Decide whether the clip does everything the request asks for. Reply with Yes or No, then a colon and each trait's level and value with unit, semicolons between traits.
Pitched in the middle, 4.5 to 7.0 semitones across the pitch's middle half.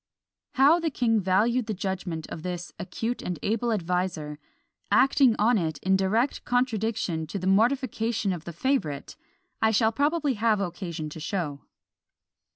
No: high, 205 Hz; average, 5.2 semitones